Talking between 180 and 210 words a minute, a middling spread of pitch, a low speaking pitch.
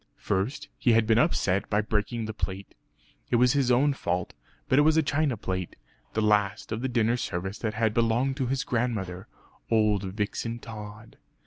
Yes: average, 185 wpm; average, 3.2 semitones; low, 110 Hz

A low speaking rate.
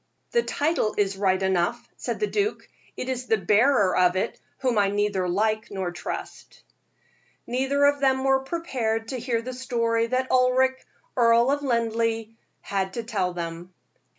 No: average, 160 wpm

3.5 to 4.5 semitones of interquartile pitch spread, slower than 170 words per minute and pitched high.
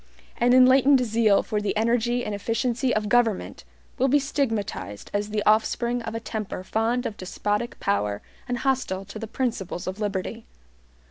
No: average, 3.1 semitones; average, 160 wpm; high, 225 Hz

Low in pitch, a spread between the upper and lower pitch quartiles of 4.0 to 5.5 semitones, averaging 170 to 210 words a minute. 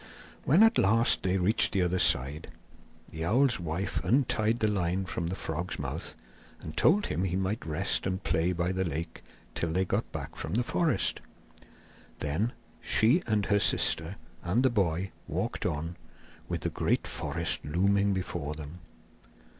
No: very low, 95 Hz; average, 4.4 semitones; average, 160 wpm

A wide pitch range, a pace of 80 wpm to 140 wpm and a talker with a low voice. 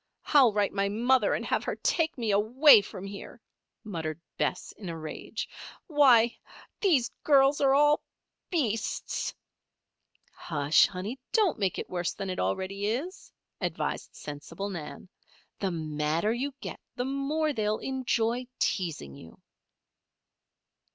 No: wide, 6.8 semitones; slow, 135 wpm; high, 215 Hz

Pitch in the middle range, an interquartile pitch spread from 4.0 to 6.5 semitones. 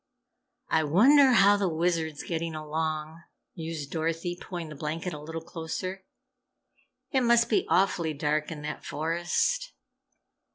No: medium, 165 Hz; average, 3.3 semitones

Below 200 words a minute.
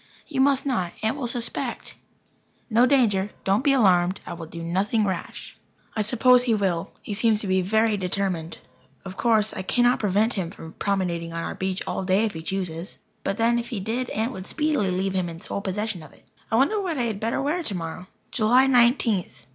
No: fast, 205 wpm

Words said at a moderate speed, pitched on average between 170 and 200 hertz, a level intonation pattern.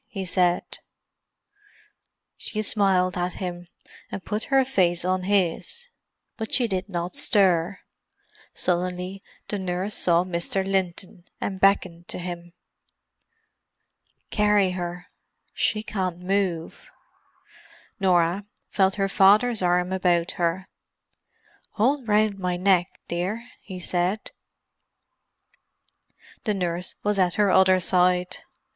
No: slow, 110 wpm; medium, 185 Hz; narrow, 2.2 semitones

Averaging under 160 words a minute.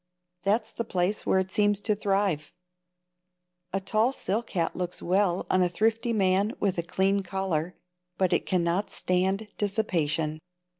Yes: average, 150 wpm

